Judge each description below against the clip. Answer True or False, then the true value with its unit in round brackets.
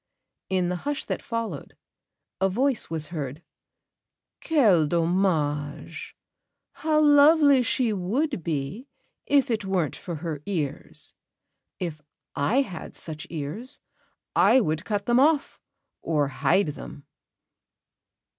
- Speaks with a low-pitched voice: False (185 Hz)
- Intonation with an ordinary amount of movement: False (8.7 semitones)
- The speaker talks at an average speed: False (115 wpm)